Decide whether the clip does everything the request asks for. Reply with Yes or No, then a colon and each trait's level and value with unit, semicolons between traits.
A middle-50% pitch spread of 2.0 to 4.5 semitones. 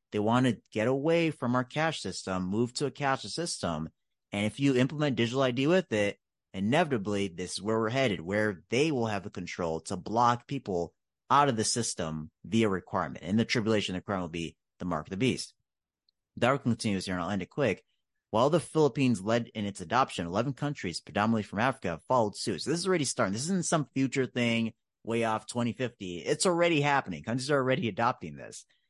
No: average, 5.2 semitones